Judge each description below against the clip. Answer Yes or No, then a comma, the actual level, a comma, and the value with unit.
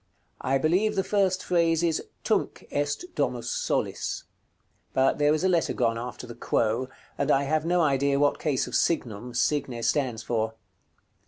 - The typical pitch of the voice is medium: Yes, medium, 145 Hz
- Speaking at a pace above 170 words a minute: No, average, 165 wpm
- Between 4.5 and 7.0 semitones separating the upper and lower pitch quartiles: Yes, average, 5.2 semitones